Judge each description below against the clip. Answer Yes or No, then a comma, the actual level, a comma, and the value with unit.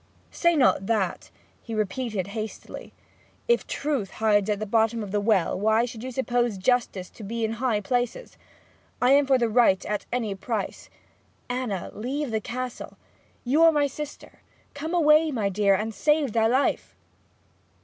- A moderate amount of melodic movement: Yes, average, 3.8 semitones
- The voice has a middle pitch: No, high, 230 Hz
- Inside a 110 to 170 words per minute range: Yes, average, 165 wpm